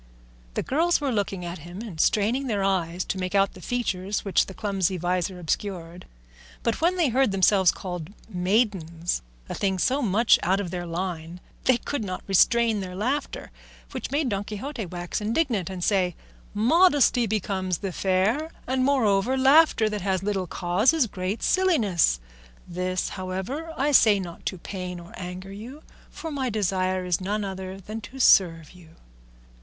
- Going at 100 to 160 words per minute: No, average, 170 wpm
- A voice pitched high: Yes, high, 195 Hz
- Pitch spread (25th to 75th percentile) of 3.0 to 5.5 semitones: Yes, average, 4.5 semitones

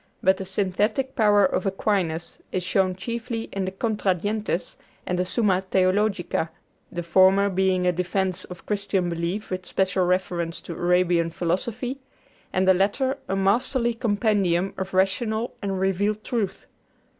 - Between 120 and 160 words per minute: Yes, average, 145 wpm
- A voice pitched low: No, high, 190 Hz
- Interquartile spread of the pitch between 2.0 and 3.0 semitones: Yes, narrow, 2.4 semitones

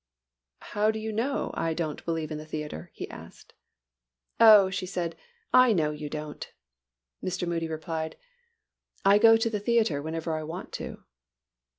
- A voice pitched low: No, medium, 170 Hz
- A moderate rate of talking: Yes, average, 160 wpm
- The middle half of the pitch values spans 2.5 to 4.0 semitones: No, average, 5.2 semitones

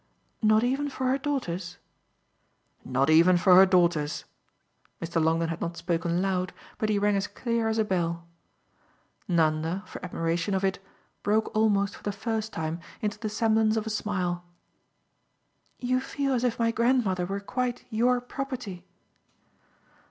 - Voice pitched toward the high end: Yes, high, 200 Hz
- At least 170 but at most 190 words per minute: No, average, 150 wpm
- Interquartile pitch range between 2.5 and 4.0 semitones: No, average, 4.7 semitones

